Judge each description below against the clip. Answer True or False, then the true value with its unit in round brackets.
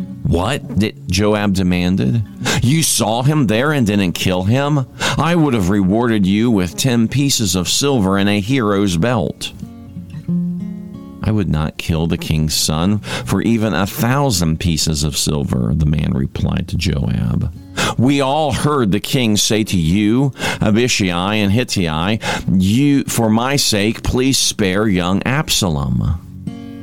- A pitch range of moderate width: False (5.9 semitones)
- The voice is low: True (105 Hz)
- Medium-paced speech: True (145 wpm)